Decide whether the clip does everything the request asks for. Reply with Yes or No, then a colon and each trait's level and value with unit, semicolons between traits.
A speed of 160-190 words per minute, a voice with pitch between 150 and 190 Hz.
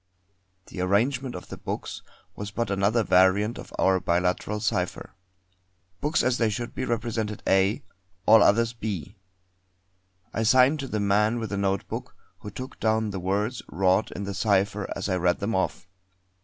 No: average, 165 wpm; low, 105 Hz